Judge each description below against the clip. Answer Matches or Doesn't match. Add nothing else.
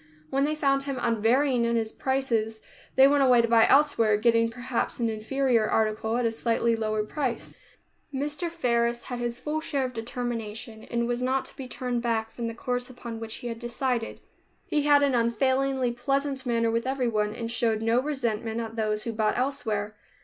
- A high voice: Matches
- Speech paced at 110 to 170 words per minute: Doesn't match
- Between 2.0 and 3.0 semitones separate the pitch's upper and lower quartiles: Matches